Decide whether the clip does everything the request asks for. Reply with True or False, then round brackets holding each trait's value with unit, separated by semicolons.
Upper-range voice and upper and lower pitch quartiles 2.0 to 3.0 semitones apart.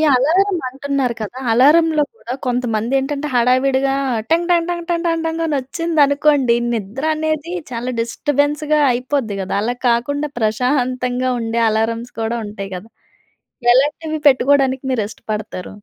False (260 Hz; 4.0 semitones)